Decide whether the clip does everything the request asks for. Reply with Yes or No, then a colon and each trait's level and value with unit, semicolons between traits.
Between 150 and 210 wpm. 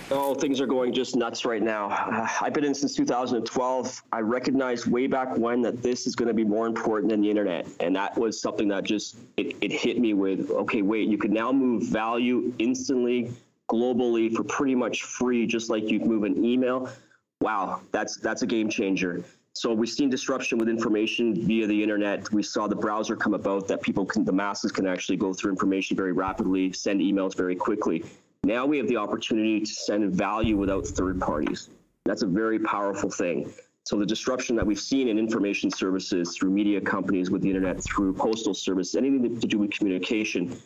Yes: average, 200 wpm